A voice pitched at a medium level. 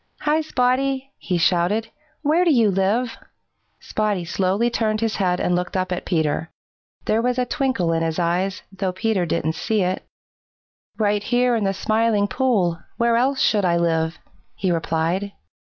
No: high, 205 Hz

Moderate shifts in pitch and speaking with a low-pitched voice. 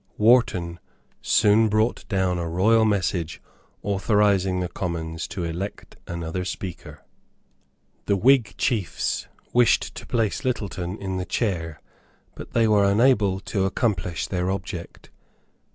Yes: average, 3.3 semitones; very low, 95 Hz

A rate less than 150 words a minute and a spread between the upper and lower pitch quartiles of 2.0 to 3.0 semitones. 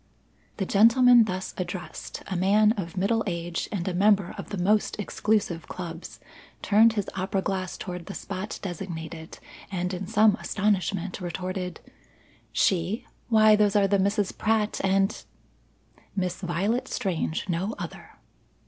Yes: average, 140 wpm; average, 2.7 semitones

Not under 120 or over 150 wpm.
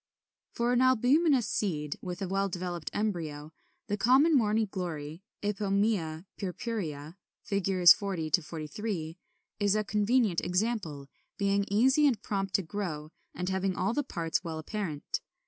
Yes: average, 145 wpm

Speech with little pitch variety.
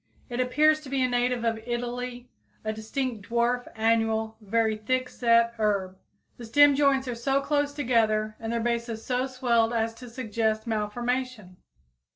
Yes: narrow, 2.3 semitones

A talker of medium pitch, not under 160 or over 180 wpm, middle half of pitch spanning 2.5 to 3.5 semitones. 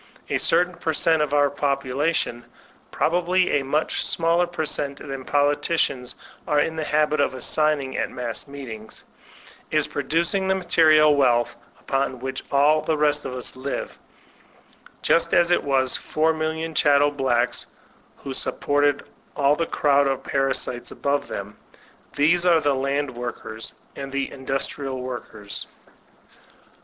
No: medium, 145 Hz; average, 145 wpm; average, 3.0 semitones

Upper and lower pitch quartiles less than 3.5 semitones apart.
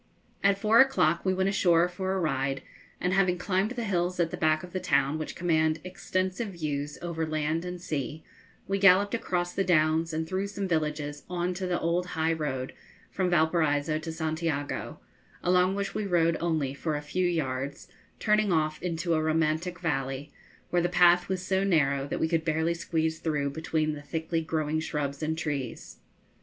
Yes: average, 2.8 semitones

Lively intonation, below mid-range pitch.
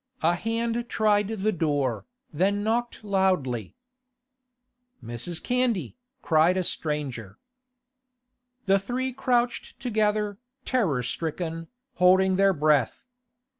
No: wide, 5.9 semitones; high, 190 Hz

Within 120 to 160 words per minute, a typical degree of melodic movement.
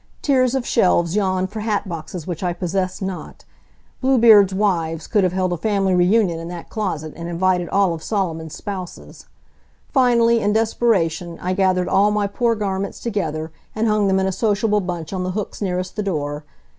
No: average, 180 wpm; average, 3.2 semitones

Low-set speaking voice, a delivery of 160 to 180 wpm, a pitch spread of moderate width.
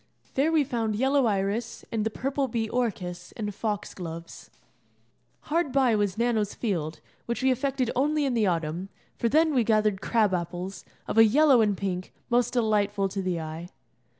No: high, 220 Hz; average, 175 wpm; average, 4.7 semitones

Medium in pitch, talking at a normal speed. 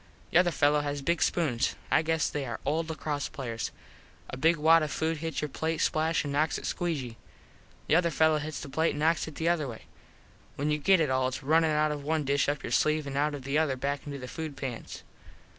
No: medium, 150 Hz; fast, 245 wpm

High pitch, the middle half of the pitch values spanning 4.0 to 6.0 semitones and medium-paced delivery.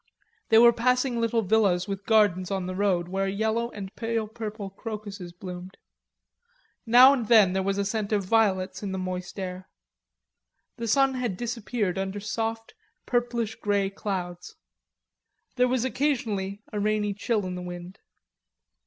No: high, 205 Hz; average, 3.2 semitones; average, 155 wpm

